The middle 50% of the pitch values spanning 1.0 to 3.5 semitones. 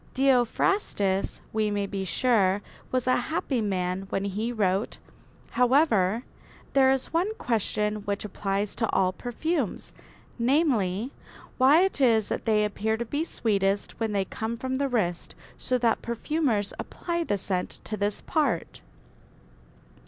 No: average, 4.6 semitones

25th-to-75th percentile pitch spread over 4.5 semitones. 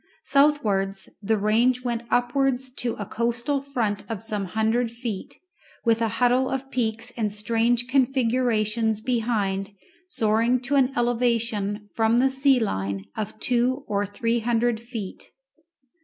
No: average, 2.7 semitones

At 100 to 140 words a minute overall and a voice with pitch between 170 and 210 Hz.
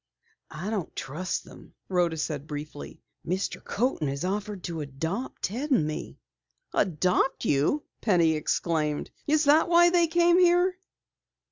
Yes: slow, 135 wpm; medium, 185 Hz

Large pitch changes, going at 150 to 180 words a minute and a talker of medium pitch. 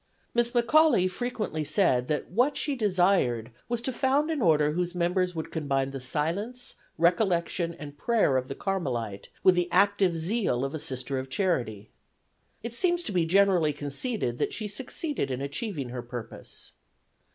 Yes: wide, 8.0 semitones; average, 165 wpm; medium, 175 Hz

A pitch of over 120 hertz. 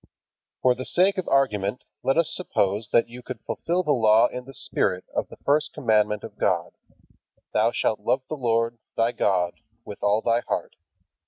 No: low, 115 Hz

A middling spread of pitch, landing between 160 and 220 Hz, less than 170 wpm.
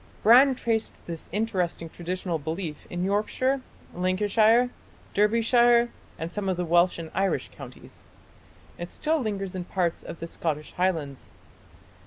Yes: average, 4.6 semitones; high, 190 Hz; slow, 135 wpm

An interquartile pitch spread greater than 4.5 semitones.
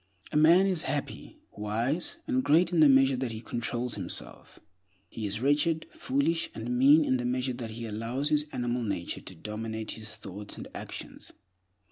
Yes: average, 5.1 semitones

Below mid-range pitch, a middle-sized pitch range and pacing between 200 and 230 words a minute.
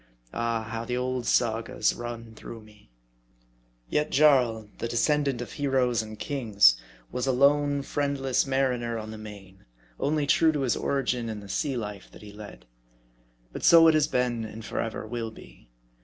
No: low, 120 Hz; average, 3.7 semitones; average, 170 wpm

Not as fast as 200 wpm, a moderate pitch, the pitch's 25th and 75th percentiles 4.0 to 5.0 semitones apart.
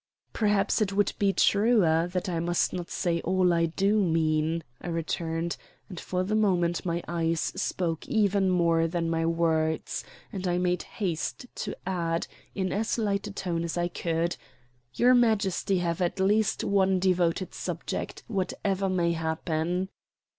No: average, 160 wpm; medium, 180 Hz; average, 2.7 semitones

